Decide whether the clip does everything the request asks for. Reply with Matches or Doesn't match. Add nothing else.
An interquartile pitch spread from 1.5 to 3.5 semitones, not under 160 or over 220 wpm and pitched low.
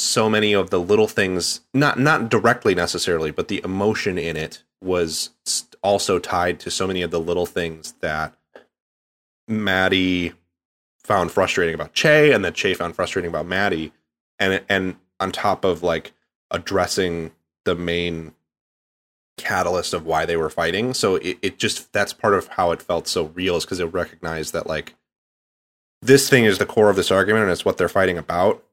Matches